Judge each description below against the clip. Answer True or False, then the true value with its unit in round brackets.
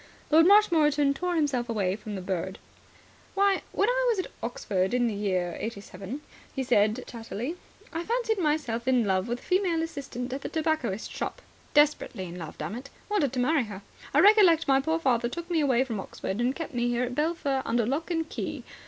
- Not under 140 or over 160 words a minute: False (195 wpm)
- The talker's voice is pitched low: False (265 Hz)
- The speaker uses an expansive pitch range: True (6.5 semitones)